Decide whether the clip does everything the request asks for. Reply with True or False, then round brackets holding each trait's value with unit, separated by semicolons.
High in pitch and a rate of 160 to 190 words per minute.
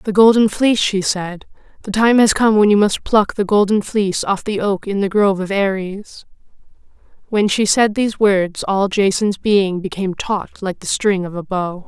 False (200 Hz; 200 wpm)